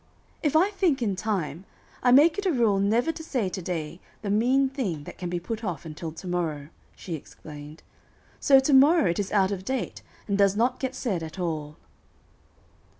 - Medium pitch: No, high, 200 Hz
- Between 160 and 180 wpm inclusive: No, average, 200 wpm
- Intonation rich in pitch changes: Yes, wide, 7.4 semitones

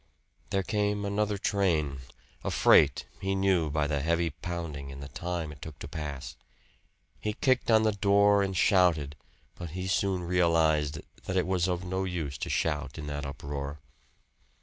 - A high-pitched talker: No, very low, 85 Hz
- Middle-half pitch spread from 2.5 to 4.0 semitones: No, average, 4.7 semitones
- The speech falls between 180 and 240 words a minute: No, average, 170 wpm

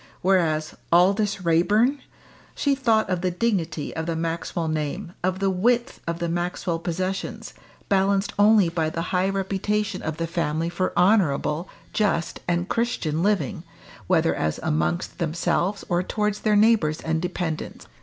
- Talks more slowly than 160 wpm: Yes, average, 145 wpm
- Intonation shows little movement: No, average, 3.5 semitones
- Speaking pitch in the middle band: Yes, medium, 180 Hz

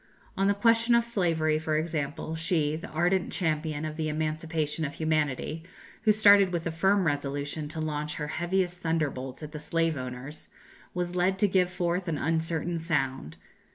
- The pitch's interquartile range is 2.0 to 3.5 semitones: Yes, average, 2.8 semitones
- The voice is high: No, medium, 160 Hz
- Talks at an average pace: Yes, average, 170 wpm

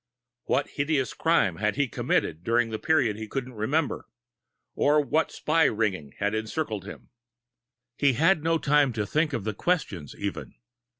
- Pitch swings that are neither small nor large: No, wide, 6.1 semitones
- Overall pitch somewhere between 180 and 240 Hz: No, low, 130 Hz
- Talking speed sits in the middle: Yes, average, 165 wpm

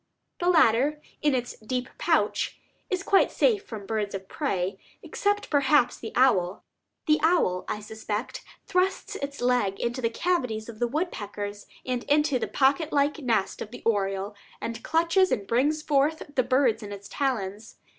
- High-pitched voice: Yes, very high, 250 Hz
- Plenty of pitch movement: Yes, wide, 6.1 semitones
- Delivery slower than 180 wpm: Yes, average, 160 wpm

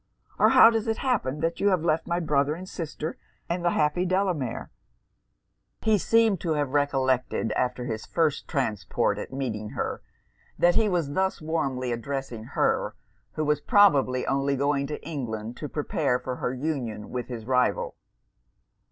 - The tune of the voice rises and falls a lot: No, average, 5.0 semitones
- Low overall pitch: No, medium, 145 Hz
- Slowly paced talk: No, average, 160 wpm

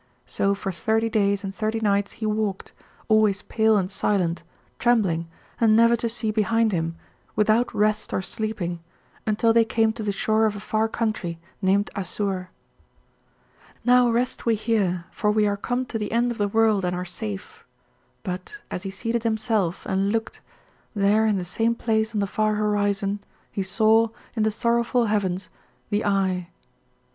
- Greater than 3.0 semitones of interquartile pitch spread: No, narrow, 2.4 semitones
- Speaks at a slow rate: No, average, 170 wpm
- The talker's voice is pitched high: Yes, high, 215 Hz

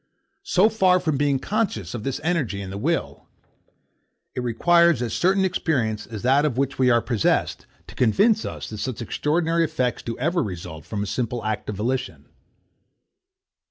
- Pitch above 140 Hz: No, low, 130 Hz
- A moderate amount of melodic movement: No, wide, 7.4 semitones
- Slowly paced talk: No, average, 170 wpm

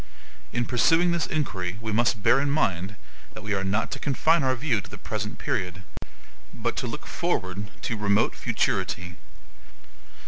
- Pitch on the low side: Yes, low, 110 Hz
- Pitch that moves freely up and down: Yes, wide, 6.0 semitones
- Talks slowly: No, average, 165 wpm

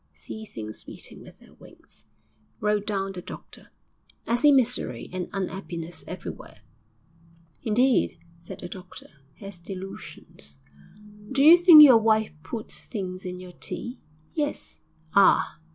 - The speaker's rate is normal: No, slow, 130 wpm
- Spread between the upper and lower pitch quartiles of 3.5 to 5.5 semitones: Yes, average, 4.9 semitones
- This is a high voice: Yes, high, 200 Hz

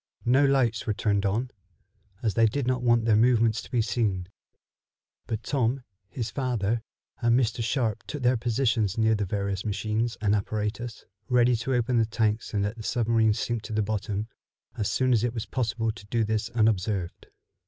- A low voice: Yes, low, 115 Hz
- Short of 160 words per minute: No, average, 185 wpm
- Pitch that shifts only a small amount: Yes, narrow, 2.2 semitones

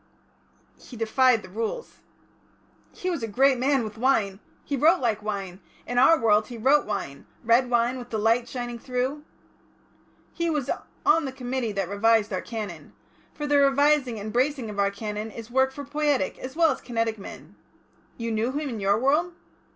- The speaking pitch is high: Yes, high, 240 Hz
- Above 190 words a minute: No, average, 180 wpm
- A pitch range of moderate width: Yes, average, 4.1 semitones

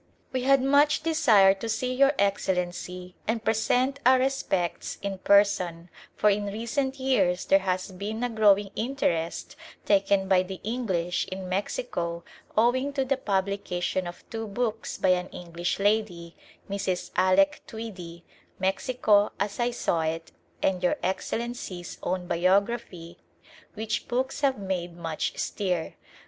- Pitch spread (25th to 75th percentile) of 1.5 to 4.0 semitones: No, average, 4.8 semitones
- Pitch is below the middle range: No, high, 200 Hz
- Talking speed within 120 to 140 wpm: Yes, slow, 135 wpm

